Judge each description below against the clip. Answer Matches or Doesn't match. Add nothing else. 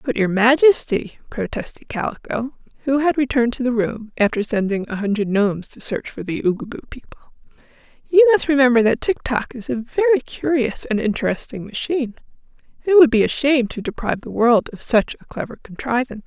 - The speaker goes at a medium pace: Matches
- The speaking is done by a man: Doesn't match